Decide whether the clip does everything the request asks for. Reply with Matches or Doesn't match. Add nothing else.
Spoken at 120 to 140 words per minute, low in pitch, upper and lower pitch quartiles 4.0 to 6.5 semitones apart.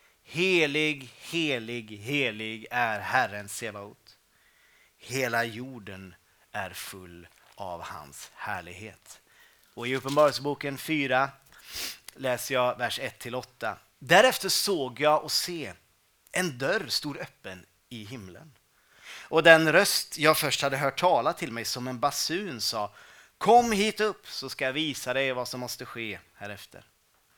Matches